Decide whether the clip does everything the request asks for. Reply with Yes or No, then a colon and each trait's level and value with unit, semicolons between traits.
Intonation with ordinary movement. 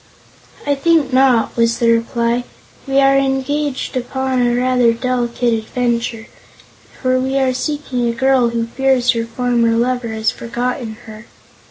No: narrow, 2.2 semitones